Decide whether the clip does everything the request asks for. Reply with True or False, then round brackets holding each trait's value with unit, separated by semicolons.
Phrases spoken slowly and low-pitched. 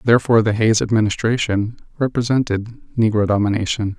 True (105 wpm; 110 Hz)